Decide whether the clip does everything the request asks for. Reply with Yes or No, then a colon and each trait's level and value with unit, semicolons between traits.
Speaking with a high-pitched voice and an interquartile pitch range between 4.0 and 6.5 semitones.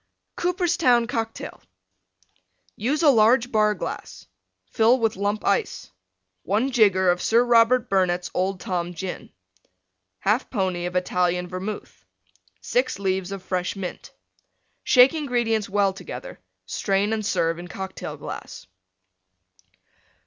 Yes: high, 205 Hz; average, 4.3 semitones